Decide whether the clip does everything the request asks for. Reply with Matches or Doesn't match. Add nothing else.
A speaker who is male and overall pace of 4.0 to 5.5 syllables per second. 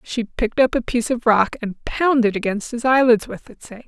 Doesn't match